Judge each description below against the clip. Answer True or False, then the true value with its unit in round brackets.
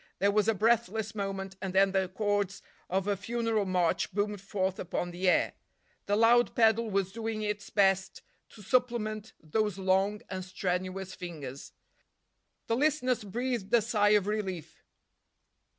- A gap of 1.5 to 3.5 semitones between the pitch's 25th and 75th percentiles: True (2.6 semitones)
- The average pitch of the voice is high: True (200 Hz)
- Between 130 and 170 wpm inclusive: True (150 wpm)